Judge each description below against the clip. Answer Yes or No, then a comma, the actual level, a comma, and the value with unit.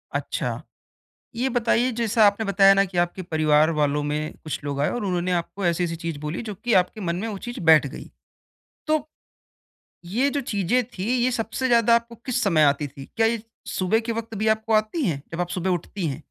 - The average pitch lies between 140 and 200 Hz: Yes, high, 190 Hz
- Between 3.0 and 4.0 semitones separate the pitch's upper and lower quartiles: No, wide, 5.6 semitones